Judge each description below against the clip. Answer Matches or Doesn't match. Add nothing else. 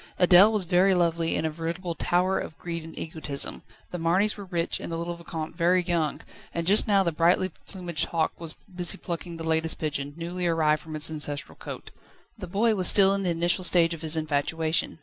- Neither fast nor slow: Doesn't match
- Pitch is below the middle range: Doesn't match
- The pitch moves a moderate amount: Doesn't match